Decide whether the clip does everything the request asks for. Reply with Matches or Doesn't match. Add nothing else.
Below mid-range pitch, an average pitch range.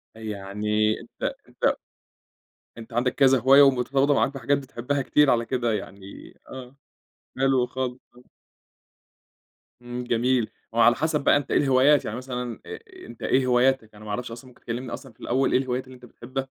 Doesn't match